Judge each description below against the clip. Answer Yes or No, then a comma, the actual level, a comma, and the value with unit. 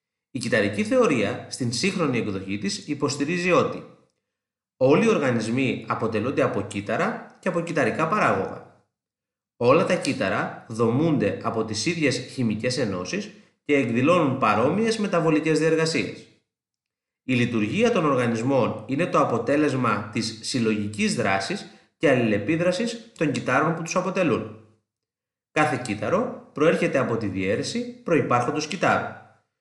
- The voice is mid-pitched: Yes, medium, 145 Hz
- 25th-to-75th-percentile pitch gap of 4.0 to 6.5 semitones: No, wide, 7.7 semitones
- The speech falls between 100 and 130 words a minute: Yes, average, 120 wpm